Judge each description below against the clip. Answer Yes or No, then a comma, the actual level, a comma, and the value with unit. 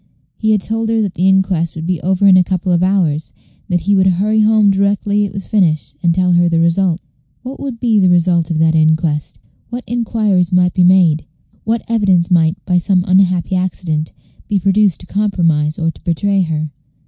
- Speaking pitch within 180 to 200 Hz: Yes, medium, 185 Hz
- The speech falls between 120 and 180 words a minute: No, fast, 205 wpm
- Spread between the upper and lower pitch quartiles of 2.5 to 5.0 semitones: Yes, average, 3.1 semitones